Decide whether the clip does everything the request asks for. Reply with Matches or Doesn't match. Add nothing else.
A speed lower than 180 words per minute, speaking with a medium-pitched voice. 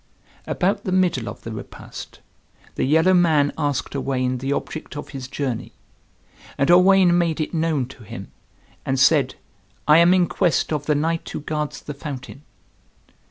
Matches